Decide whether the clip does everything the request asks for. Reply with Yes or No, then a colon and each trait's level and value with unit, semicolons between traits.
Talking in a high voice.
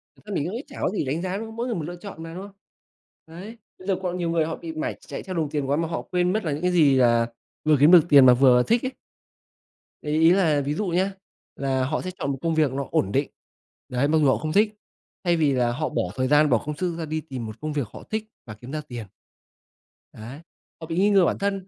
No: medium, 155 Hz